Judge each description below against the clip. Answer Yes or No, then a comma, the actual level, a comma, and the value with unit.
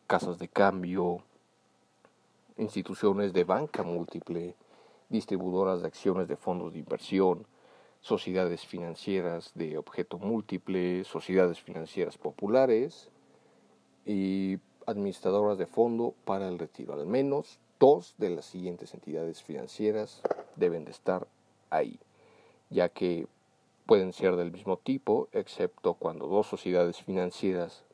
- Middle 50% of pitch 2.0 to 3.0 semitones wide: Yes, narrow, 2.4 semitones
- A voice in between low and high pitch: No, very low, 95 Hz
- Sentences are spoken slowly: Yes, slow, 115 wpm